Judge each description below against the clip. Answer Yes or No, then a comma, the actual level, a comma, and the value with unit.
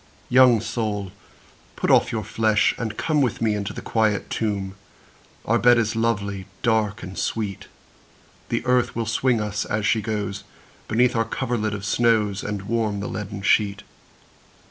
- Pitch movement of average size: No, narrow, 2.1 semitones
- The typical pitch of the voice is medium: No, low, 110 Hz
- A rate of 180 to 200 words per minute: No, average, 165 wpm